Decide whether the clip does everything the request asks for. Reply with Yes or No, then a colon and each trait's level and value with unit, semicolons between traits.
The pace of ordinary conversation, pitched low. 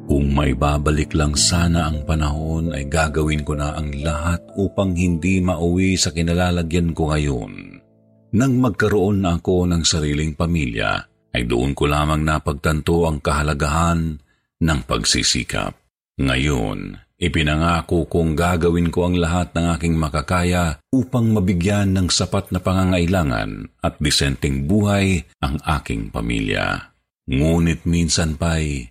Yes: average, 125 wpm; very low, 85 Hz